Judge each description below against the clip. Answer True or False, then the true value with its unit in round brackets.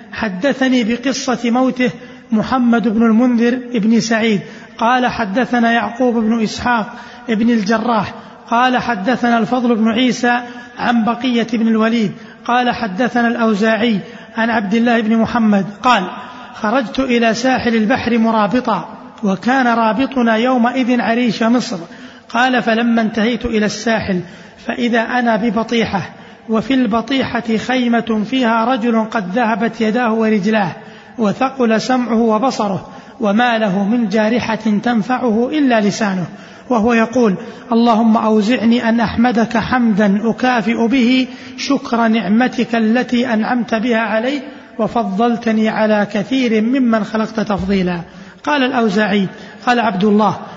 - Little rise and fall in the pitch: True (1.8 semitones)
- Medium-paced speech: True (115 wpm)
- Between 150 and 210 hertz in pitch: False (230 Hz)